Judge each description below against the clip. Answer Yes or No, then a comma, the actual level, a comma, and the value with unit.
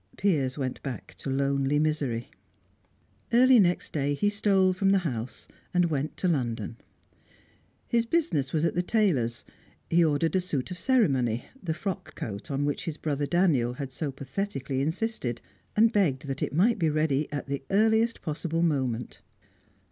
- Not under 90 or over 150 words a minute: No, average, 165 wpm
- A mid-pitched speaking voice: Yes, medium, 155 Hz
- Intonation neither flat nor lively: No, wide, 5.8 semitones